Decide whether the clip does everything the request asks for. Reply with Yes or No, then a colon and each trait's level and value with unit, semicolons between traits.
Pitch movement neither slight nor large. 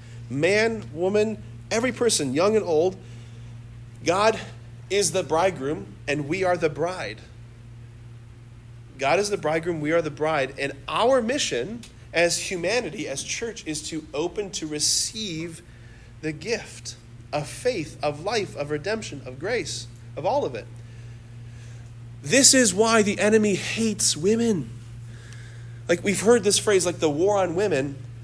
No: wide, 7.8 semitones